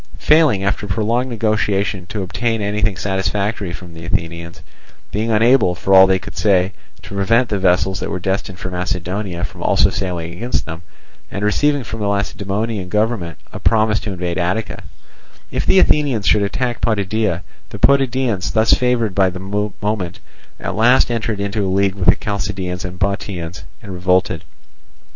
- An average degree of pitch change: Yes, average, 3.1 semitones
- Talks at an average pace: Yes, average, 160 wpm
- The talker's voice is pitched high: No, low, 100 Hz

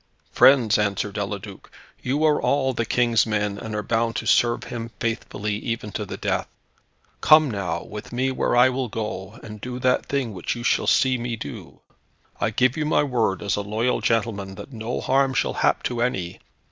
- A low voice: Yes, low, 115 Hz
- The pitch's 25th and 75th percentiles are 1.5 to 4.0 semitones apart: Yes, average, 3.2 semitones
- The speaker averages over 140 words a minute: Yes, average, 195 wpm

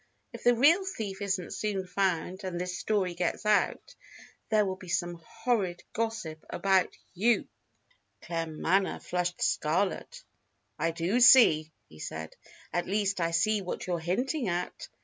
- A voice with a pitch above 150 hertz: Yes, medium, 185 Hz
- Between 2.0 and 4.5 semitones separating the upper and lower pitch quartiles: Yes, average, 3.7 semitones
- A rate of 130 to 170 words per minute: Yes, average, 145 wpm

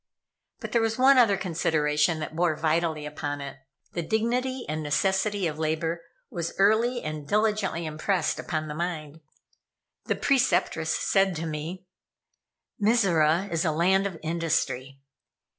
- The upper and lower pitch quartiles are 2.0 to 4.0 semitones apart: No, average, 4.4 semitones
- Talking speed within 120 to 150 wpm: Yes, average, 140 wpm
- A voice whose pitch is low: No, medium, 170 Hz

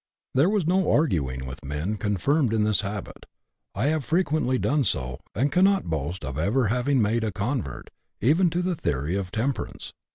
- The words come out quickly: No, average, 175 wpm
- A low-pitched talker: Yes, low, 115 Hz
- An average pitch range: No, wide, 8.5 semitones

